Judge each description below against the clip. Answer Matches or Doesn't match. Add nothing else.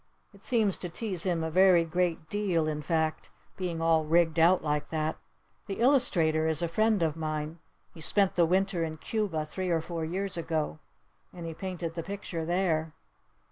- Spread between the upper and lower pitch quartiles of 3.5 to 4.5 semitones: Doesn't match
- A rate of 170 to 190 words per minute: Matches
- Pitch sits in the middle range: Matches